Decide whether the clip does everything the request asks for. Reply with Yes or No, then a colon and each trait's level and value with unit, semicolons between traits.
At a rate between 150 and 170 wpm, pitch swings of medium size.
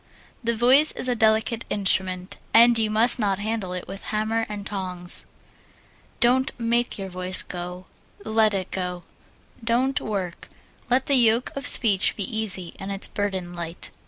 Yes: average, 160 wpm; average, 3.8 semitones